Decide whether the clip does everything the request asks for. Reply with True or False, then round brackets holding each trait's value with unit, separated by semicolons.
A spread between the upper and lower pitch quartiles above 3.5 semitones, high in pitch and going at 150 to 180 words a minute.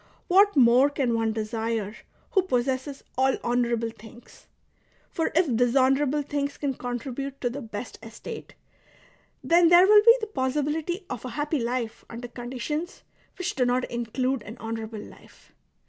True (3.9 semitones; 255 Hz; 155 wpm)